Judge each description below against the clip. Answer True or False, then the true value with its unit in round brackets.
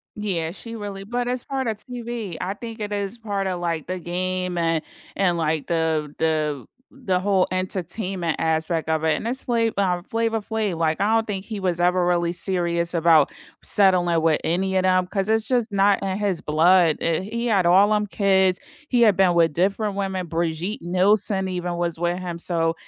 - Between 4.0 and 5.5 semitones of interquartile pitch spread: False (3.4 semitones)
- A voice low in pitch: False (185 Hz)